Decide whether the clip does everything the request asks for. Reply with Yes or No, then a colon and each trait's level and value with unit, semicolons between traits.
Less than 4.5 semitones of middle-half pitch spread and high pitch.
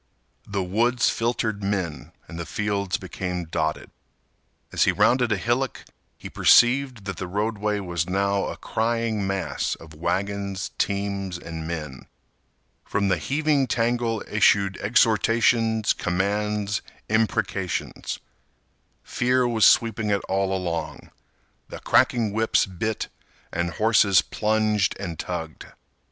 No: average, 3.3 semitones; low, 100 Hz